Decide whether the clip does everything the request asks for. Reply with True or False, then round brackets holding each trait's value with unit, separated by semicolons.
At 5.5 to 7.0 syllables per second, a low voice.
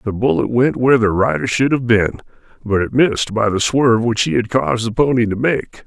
True (5.8 syllables/s; 115 Hz)